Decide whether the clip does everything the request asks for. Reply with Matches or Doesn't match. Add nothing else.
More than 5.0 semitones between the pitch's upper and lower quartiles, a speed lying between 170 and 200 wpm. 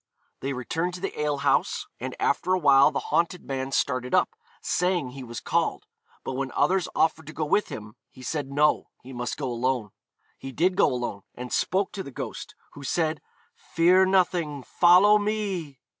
Matches